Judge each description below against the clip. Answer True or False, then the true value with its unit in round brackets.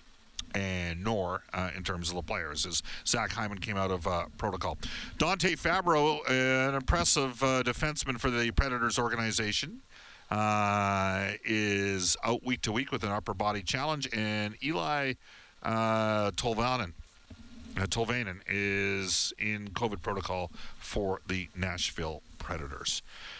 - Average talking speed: False (130 wpm)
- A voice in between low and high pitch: False (105 Hz)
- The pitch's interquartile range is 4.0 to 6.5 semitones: True (4.9 semitones)